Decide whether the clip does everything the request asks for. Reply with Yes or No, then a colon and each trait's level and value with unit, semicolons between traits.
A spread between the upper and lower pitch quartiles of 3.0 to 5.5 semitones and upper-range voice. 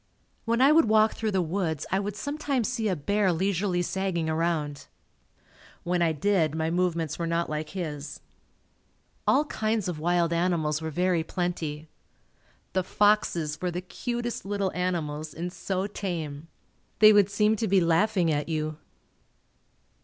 No: average, 4.2 semitones; medium, 180 Hz